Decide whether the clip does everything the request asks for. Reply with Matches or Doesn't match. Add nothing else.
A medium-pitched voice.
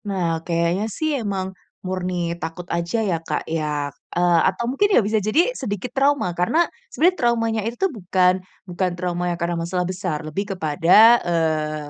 Matches